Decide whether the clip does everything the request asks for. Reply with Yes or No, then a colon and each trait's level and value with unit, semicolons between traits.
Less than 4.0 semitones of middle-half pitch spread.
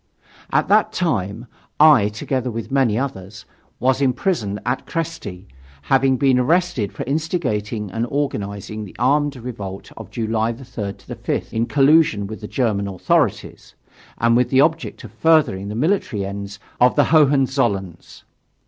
No: average, 5.3 semitones